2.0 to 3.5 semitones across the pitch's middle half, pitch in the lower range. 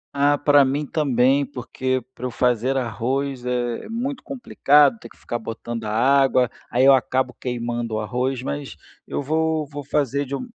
Yes: average, 2.9 semitones; low, 130 Hz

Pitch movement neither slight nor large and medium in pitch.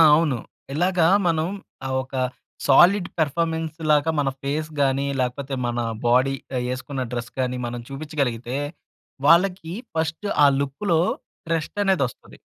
Yes: average, 3.8 semitones; medium, 145 Hz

